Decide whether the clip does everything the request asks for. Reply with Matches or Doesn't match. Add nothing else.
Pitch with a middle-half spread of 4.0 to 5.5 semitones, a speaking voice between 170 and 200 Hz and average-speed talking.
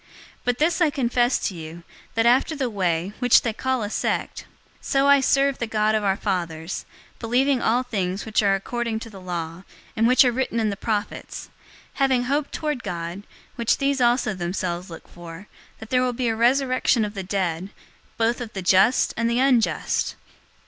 Doesn't match